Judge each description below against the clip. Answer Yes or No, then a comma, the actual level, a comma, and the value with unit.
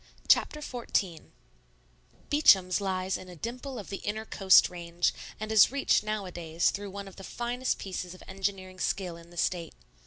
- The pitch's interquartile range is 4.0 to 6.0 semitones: No, average, 3.1 semitones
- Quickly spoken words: No, average, 165 wpm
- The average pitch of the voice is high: Yes, high, 195 Hz